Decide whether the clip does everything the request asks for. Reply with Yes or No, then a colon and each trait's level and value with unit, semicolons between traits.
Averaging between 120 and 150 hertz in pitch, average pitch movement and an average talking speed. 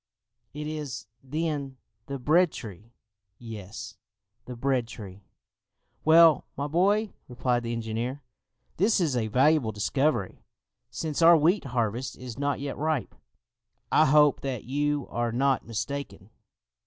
No: low, 135 Hz; average, 4.5 semitones; slow, 130 wpm